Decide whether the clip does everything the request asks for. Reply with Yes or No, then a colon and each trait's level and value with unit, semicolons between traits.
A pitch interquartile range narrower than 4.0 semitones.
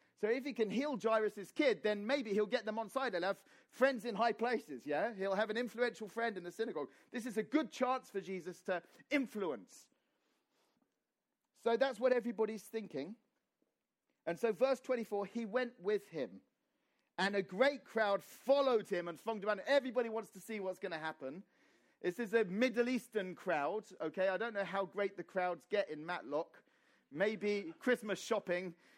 No: average, 4.3 semitones